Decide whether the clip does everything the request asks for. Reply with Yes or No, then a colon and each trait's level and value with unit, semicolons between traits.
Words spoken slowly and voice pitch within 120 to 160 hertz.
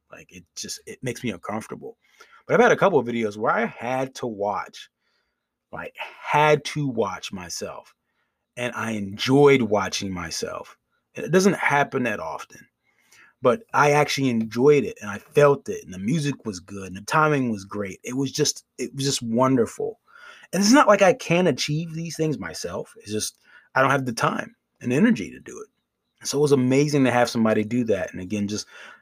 No: average, 195 wpm; medium, 140 Hz